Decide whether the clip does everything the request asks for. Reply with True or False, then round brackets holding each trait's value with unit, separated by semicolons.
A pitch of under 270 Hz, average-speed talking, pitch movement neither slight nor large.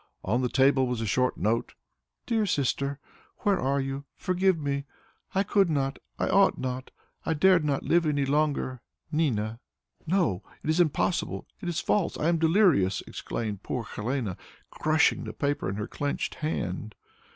True (140 Hz; 165 wpm; 4.9 semitones)